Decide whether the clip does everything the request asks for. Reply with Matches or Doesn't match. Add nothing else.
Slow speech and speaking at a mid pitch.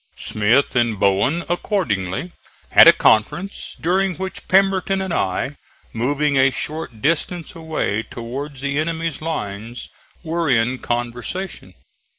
Matches